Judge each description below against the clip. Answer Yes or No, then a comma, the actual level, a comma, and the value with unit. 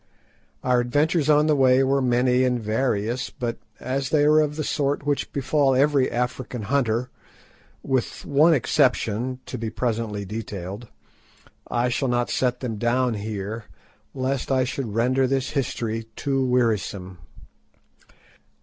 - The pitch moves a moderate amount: Yes, average, 3.0 semitones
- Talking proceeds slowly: Yes, slow, 130 wpm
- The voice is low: Yes, low, 125 Hz